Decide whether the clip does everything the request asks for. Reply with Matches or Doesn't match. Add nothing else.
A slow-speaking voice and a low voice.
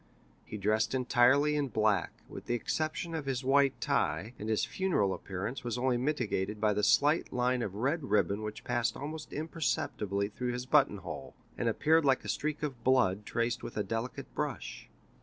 Doesn't match